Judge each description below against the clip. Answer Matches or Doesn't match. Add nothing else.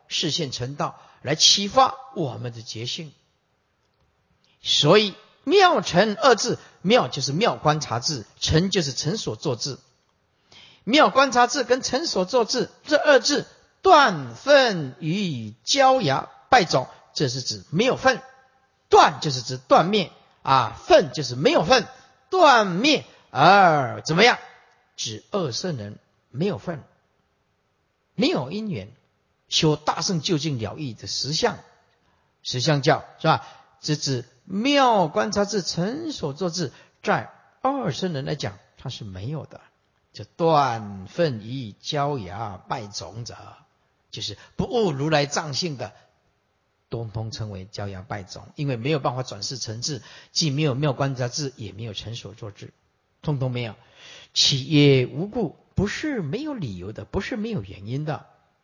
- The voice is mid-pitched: Matches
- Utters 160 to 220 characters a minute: Matches